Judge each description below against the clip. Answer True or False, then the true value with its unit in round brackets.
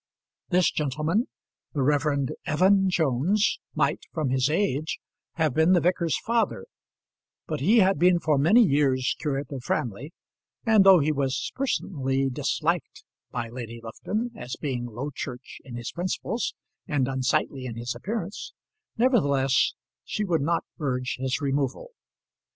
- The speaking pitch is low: False (145 Hz)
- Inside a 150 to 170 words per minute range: False (140 wpm)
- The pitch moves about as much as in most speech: False (5.8 semitones)